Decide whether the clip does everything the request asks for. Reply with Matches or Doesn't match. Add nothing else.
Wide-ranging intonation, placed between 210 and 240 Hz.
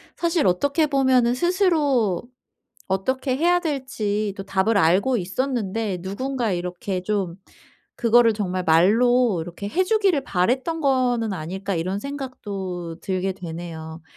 Matches